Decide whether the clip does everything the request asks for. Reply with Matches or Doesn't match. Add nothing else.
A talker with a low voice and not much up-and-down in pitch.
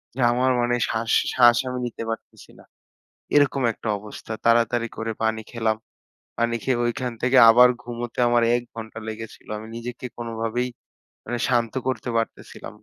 Matches